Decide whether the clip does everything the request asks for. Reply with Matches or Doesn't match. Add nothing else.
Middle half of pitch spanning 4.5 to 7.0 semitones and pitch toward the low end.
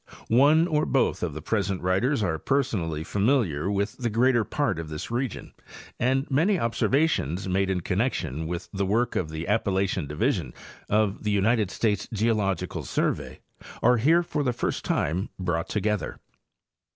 Matches